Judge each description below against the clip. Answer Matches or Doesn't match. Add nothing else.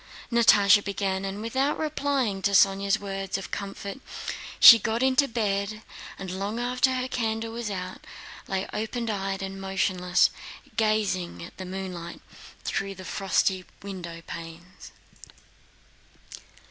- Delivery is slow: Matches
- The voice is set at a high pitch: Matches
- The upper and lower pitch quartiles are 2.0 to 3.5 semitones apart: Matches